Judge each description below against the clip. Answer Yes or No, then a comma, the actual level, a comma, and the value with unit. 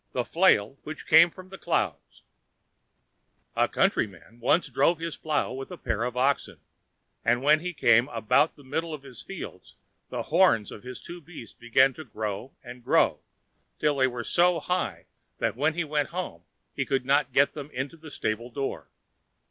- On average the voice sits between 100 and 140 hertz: Yes, low, 135 Hz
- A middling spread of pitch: Yes, average, 4.7 semitones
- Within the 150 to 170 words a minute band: No, average, 180 wpm